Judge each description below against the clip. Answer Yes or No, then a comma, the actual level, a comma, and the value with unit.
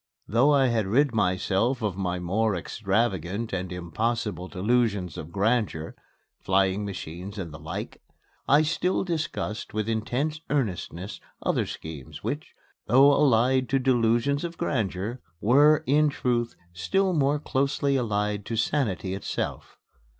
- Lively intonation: Yes, wide, 6.0 semitones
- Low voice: Yes, low, 115 Hz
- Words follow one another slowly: Yes, slow, 130 wpm